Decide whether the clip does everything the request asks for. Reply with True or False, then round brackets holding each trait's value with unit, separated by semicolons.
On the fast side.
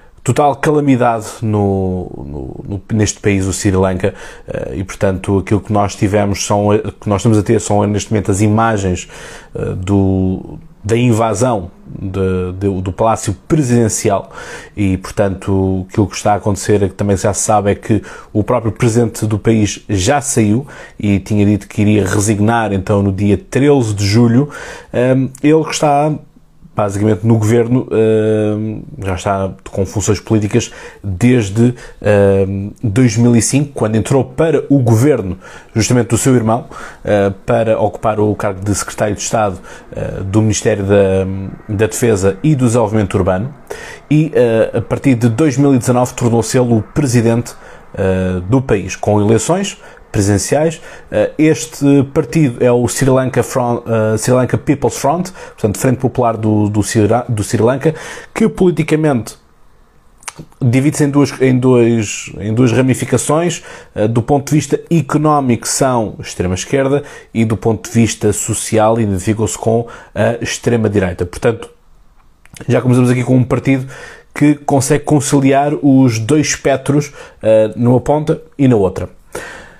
False (140 wpm)